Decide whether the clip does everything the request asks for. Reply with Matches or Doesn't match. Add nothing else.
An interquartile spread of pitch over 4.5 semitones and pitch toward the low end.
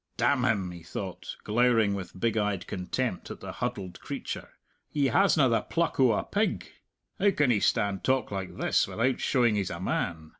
Matches